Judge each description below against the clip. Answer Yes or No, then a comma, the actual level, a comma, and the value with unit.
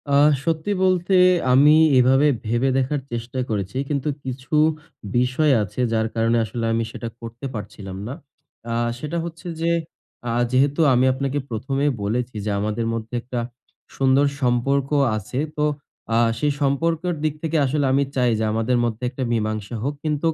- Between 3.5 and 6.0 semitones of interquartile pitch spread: Yes, average, 3.9 semitones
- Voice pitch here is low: Yes, low, 130 Hz